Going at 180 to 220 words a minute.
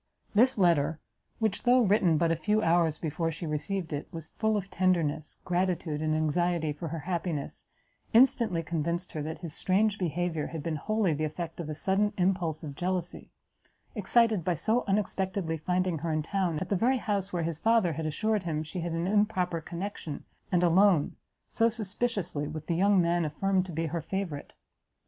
Yes: average, 185 wpm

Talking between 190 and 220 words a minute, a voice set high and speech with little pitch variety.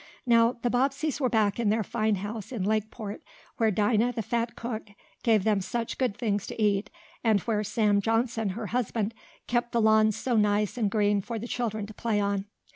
Yes: average, 200 wpm; high, 220 Hz; narrow, 2.2 semitones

